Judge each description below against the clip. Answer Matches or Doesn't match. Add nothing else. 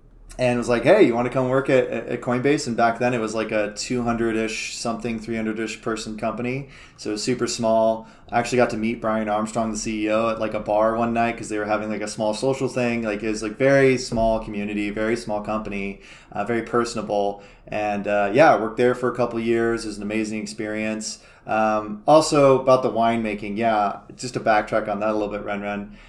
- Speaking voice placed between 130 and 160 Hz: Doesn't match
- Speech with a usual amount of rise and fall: Doesn't match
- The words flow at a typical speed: Doesn't match